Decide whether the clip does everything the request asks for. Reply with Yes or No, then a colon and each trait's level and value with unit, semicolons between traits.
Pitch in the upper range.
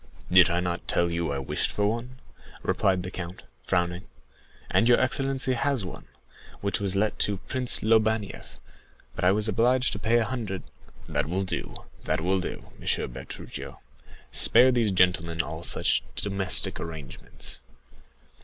No: low, 100 Hz